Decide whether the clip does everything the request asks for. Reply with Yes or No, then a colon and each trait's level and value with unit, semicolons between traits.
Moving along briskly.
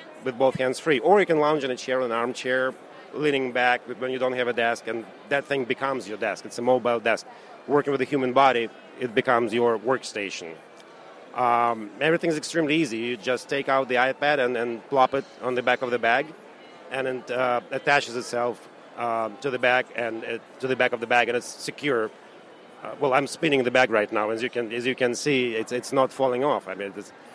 Yes: fast, 230 wpm